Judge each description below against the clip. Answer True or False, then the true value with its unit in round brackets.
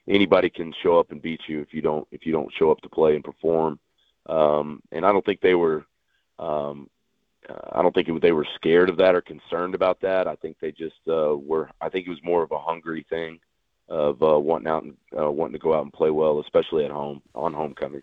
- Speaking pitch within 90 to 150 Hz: False (80 Hz)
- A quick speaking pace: True (245 wpm)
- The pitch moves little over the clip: True (1.7 semitones)